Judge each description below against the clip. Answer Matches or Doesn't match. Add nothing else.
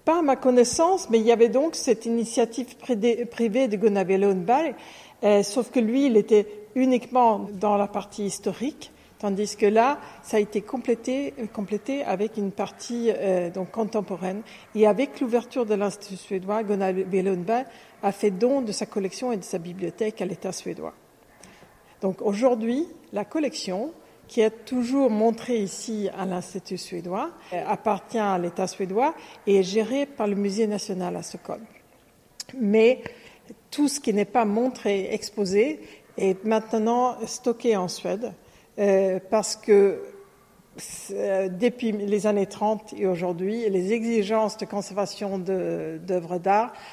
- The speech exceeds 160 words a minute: Doesn't match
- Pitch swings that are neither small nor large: Matches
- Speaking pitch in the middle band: Doesn't match